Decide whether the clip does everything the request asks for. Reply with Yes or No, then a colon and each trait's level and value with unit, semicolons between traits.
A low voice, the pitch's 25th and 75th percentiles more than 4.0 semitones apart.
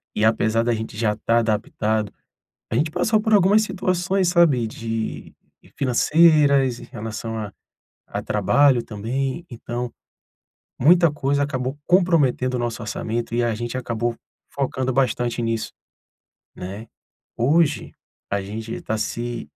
Yes: low, 120 Hz; average, 4.4 semitones